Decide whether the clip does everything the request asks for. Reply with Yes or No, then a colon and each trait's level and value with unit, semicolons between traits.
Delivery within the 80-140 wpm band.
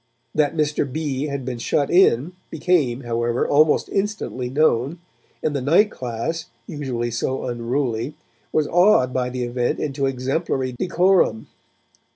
Yes: slow, 135 wpm